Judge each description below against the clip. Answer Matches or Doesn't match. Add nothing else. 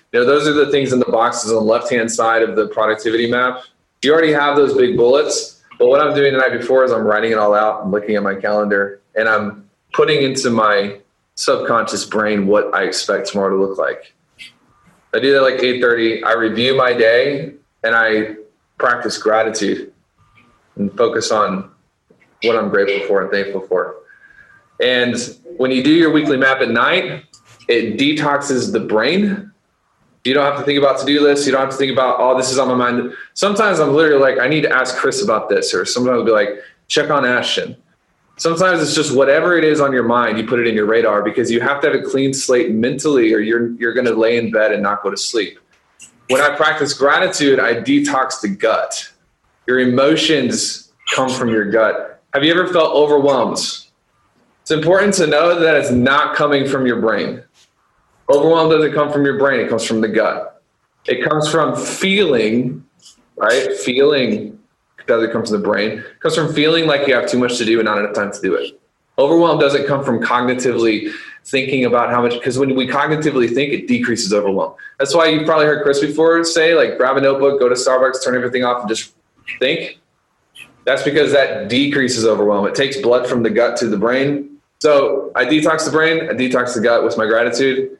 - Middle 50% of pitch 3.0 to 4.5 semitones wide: Doesn't match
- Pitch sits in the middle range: Doesn't match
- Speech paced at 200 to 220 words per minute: Matches